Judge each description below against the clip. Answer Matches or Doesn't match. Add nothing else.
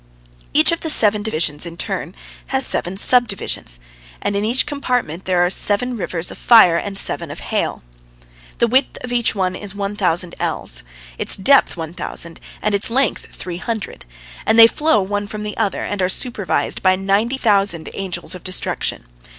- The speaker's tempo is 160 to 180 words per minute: Matches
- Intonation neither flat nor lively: Matches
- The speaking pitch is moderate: Doesn't match